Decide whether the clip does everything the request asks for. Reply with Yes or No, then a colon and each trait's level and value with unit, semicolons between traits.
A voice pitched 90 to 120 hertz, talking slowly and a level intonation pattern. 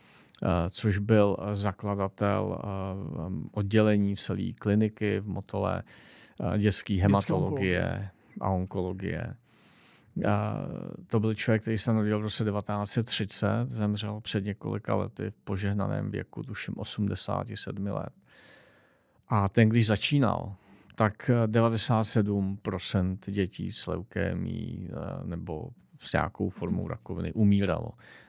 Yes: low, 105 Hz; slow, 110 wpm; narrow, 1.9 semitones